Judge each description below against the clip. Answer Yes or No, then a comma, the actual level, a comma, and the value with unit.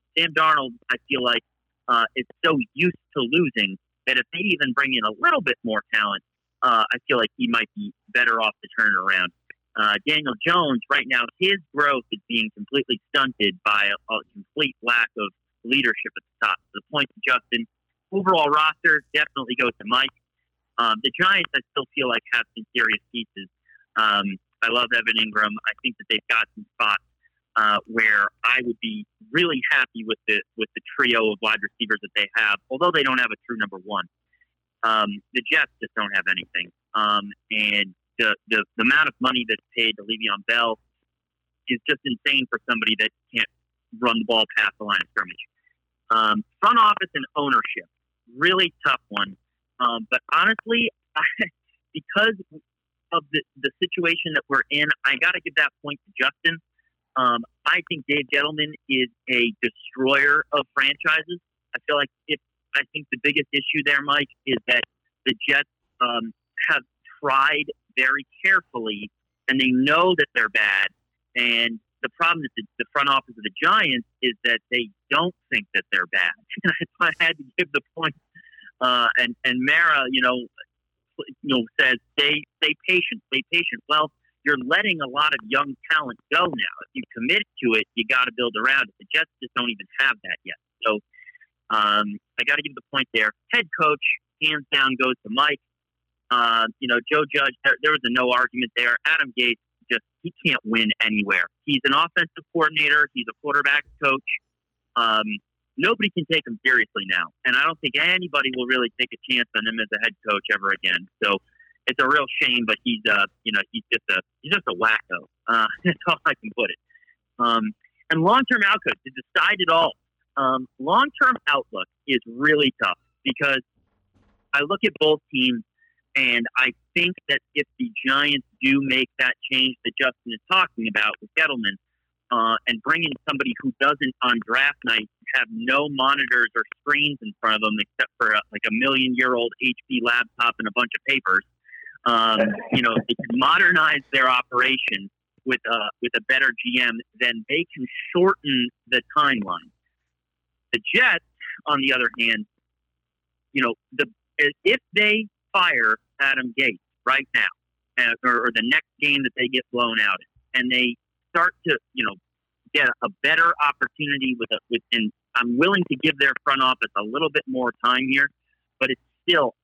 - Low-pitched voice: Yes, low, 130 Hz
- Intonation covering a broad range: Yes, wide, 6.2 semitones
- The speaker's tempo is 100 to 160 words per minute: No, average, 185 wpm